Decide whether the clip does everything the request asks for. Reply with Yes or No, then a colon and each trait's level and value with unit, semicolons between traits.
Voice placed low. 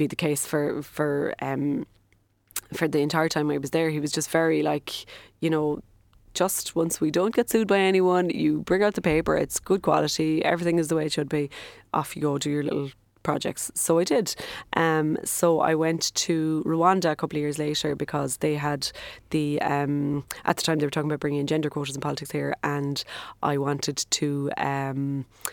No: medium, 150 Hz